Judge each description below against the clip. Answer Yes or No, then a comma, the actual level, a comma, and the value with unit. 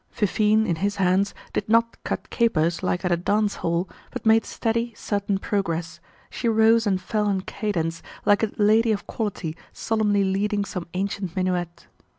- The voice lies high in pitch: Yes, high, 200 Hz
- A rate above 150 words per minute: Yes, average, 165 wpm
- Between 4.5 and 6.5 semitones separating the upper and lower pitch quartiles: No, average, 3.1 semitones